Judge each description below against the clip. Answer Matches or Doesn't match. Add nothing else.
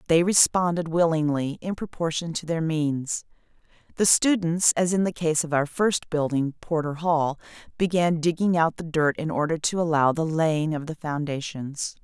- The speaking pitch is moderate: Matches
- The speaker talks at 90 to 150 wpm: Doesn't match